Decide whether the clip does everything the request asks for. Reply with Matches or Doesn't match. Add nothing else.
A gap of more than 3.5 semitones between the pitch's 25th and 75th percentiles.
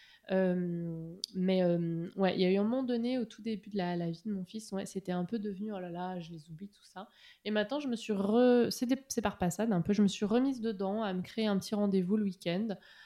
Doesn't match